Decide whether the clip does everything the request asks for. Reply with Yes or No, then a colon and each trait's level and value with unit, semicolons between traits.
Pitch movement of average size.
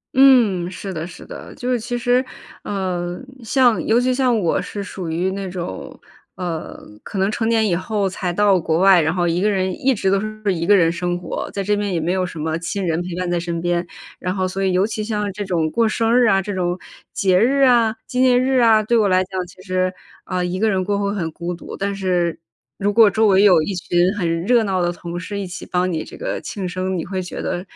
Yes: average, 3.2 semitones